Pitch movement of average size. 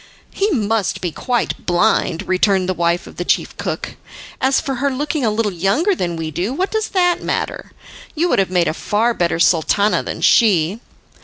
No: wide, 7.3 semitones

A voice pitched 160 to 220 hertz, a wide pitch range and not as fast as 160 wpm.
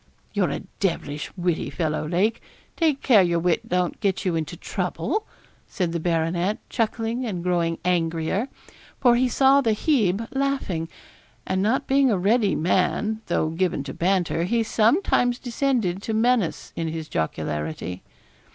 Yes: medium, 185 Hz; wide, 5.8 semitones; average, 150 wpm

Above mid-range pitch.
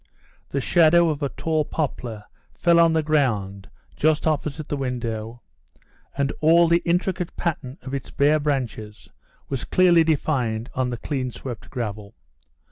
No: medium, 140 Hz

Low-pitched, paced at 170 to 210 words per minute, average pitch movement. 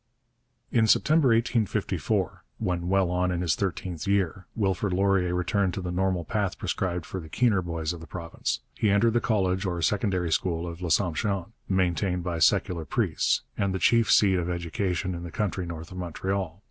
No: very low, 90 Hz; average, 180 wpm; narrow, 2.3 semitones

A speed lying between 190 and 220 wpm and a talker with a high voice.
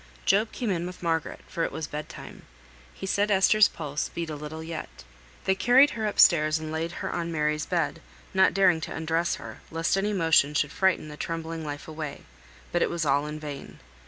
No: fast, 205 wpm; medium, 165 Hz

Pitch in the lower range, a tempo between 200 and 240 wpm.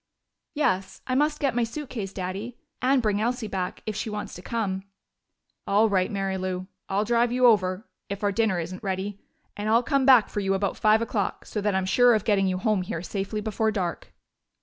No: high, 210 Hz; fast, 205 wpm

